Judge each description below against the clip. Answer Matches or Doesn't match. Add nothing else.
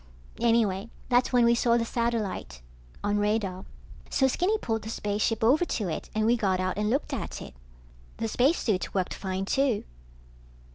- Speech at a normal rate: Matches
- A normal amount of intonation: Matches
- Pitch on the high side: Matches